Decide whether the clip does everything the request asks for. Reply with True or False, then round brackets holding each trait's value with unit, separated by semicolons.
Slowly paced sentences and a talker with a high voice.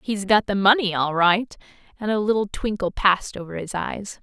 False (200 wpm; 200 Hz)